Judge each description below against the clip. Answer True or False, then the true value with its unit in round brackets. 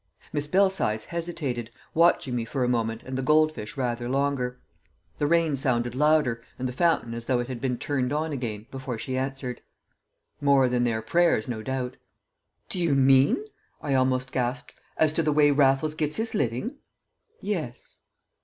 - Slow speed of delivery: False (170 wpm)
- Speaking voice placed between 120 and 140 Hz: True (135 Hz)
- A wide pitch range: False (3.7 semitones)